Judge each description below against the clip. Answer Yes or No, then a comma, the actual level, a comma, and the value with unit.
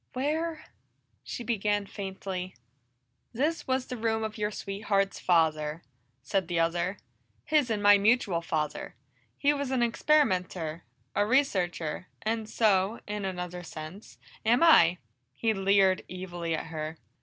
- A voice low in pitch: No, high, 200 Hz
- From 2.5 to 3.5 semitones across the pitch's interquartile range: No, average, 4.6 semitones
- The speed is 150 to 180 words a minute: No, slow, 135 wpm